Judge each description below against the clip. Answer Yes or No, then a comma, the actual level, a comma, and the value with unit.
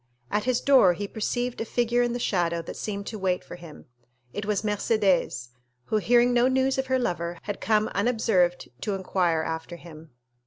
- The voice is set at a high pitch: Yes, high, 205 Hz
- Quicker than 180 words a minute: Yes, average, 190 wpm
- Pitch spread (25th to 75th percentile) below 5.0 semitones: No, wide, 5.4 semitones